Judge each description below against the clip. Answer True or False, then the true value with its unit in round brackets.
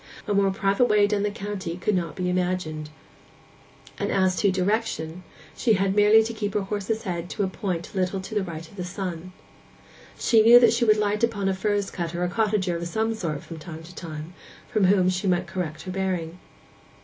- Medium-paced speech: False (210 wpm)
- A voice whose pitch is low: False (190 Hz)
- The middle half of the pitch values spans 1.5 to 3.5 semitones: True (2.9 semitones)